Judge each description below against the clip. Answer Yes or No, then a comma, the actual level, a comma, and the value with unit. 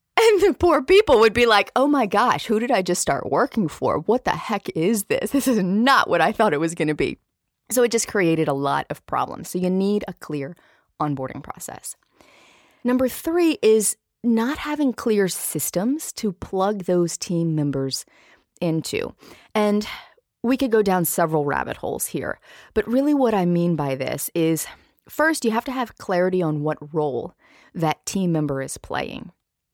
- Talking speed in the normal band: Yes, average, 185 wpm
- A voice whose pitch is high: Yes, high, 205 Hz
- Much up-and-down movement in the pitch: Yes, wide, 7.2 semitones